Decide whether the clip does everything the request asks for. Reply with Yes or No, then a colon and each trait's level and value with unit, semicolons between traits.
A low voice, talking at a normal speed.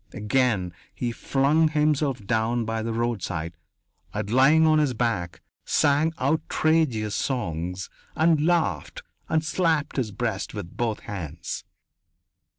No: low, 120 Hz; slow, 120 wpm